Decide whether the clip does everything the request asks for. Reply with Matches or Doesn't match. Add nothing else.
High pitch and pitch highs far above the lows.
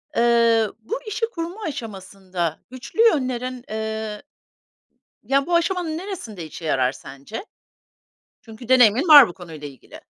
Matches